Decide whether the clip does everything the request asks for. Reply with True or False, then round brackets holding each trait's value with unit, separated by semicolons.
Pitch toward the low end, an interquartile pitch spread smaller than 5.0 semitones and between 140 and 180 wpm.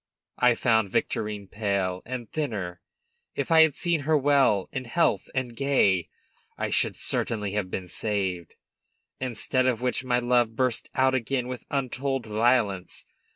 True (120 Hz; 4.2 semitones; 150 wpm)